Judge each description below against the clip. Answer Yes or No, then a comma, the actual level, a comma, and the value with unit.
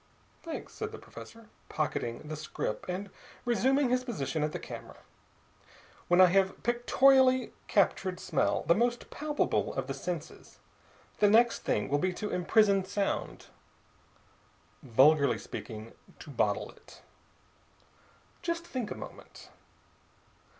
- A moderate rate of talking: No, slow, 125 wpm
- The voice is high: Yes, high, 195 Hz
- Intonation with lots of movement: Yes, wide, 7.8 semitones